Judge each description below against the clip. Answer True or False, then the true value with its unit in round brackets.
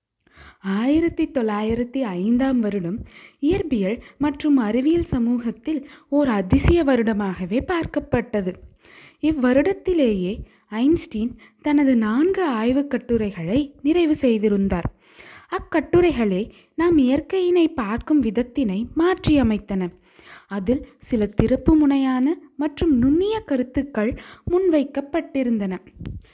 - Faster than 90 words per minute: False (75 wpm)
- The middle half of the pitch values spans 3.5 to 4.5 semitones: False (5.6 semitones)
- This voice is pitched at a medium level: False (265 Hz)